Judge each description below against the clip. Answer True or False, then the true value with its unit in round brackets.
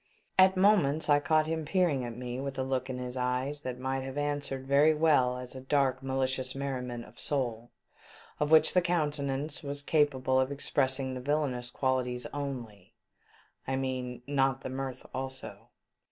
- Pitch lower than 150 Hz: True (135 Hz)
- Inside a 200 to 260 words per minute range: False (170 wpm)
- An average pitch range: False (2.2 semitones)